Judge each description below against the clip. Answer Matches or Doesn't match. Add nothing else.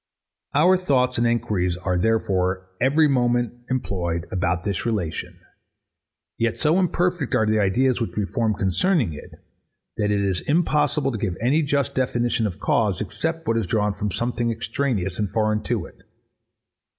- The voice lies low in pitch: Matches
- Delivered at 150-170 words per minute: Matches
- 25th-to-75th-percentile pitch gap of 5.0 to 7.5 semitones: Matches